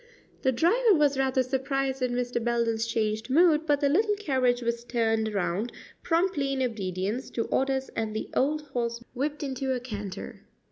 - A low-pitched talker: No, very high, 255 Hz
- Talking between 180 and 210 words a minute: No, average, 170 wpm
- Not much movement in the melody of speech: No, average, 3.4 semitones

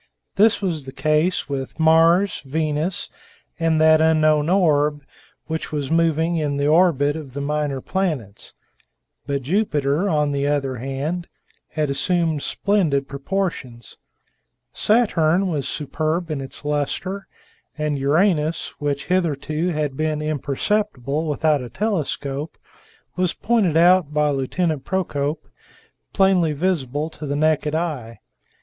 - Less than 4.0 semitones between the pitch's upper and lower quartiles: Yes, average, 3.2 semitones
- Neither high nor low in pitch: Yes, medium, 155 Hz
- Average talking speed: No, slow, 125 wpm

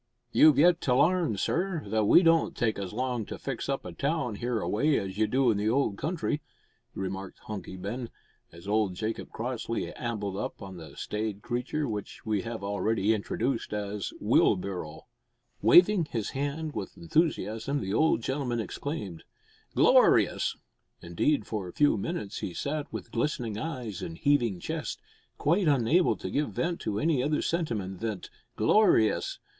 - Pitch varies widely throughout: Yes, wide, 6.3 semitones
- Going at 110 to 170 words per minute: Yes, average, 160 wpm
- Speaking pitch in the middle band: No, low, 115 Hz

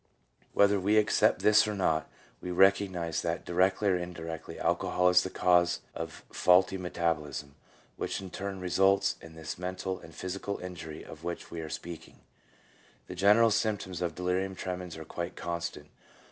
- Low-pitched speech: Yes, very low, 90 Hz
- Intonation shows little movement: Yes, narrow, 2.3 semitones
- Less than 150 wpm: No, average, 160 wpm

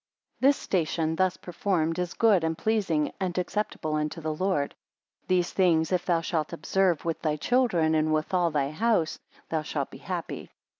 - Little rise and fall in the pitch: No, average, 3.1 semitones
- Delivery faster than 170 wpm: Yes, average, 180 wpm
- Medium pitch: Yes, medium, 170 Hz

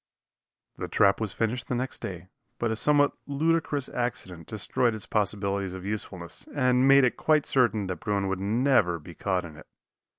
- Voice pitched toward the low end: Yes, low, 110 Hz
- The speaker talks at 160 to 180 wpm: Yes, average, 175 wpm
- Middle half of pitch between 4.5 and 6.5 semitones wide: Yes, average, 4.9 semitones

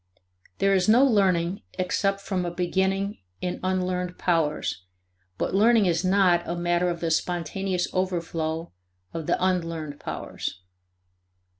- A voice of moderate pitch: Yes, medium, 180 Hz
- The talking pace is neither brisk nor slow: No, slow, 130 wpm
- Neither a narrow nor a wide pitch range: No, narrow, 2.2 semitones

